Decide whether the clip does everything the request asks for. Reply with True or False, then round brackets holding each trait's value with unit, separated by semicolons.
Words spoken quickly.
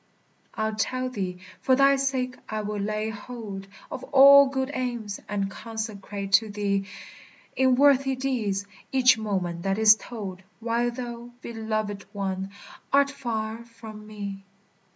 False (135 wpm)